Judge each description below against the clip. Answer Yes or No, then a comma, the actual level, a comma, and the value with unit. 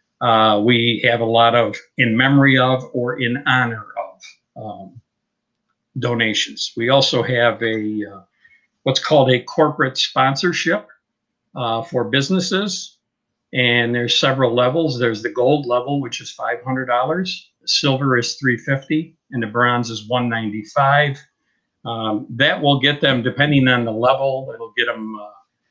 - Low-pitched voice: Yes, low, 125 Hz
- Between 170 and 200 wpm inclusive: No, average, 140 wpm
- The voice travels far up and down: No, average, 2.9 semitones